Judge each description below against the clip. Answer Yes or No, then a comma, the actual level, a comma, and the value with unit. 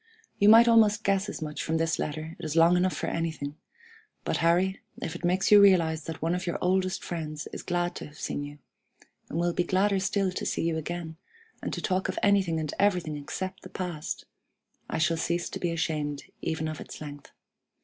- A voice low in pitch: No, medium, 170 Hz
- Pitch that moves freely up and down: No, average, 3.0 semitones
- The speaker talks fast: Yes, fast, 210 wpm